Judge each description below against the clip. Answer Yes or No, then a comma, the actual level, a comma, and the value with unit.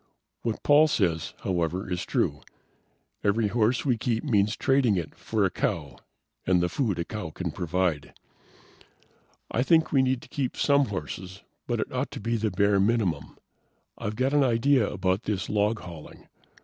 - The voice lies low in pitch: Yes, low, 105 Hz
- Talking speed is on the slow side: No, average, 170 wpm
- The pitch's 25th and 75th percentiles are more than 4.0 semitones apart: Yes, average, 5.1 semitones